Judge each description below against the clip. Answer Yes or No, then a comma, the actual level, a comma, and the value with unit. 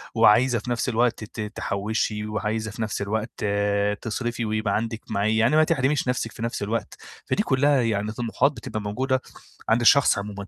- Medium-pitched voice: No, low, 115 Hz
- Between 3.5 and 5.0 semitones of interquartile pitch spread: No, average, 2.7 semitones